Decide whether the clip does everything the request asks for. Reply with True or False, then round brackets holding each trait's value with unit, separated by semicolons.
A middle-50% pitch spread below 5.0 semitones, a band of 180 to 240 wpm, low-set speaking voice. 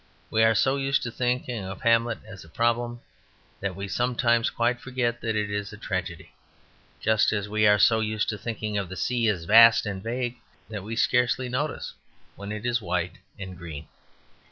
True (2.9 semitones; 190 wpm; 110 Hz)